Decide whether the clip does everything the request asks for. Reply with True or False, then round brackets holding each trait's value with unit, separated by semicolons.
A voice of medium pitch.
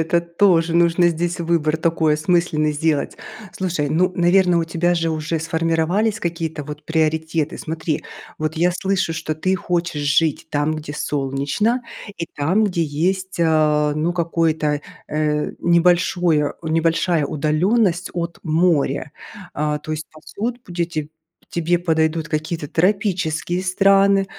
True (165 Hz)